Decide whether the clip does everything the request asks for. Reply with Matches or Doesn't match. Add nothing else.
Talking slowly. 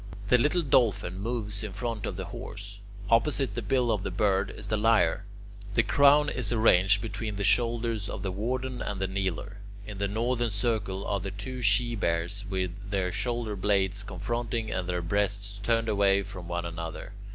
Doesn't match